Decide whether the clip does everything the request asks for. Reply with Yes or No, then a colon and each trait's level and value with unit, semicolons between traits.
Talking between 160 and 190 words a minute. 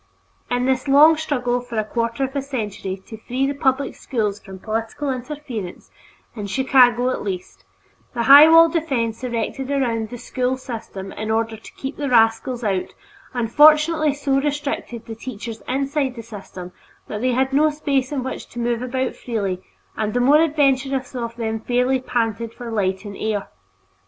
Yes: average, 175 wpm